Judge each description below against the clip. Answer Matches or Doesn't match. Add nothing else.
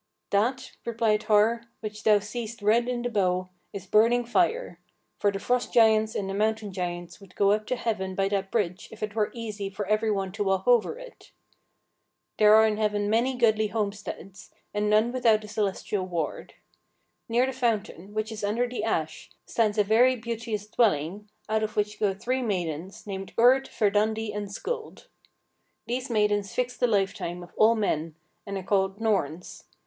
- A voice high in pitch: Matches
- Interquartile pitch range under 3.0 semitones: Matches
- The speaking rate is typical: Matches